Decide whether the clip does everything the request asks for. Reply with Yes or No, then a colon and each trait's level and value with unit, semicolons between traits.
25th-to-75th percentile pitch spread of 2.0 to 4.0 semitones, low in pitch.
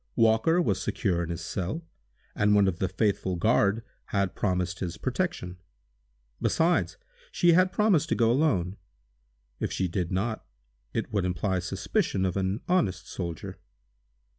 No: average, 4.8 semitones; low, 100 Hz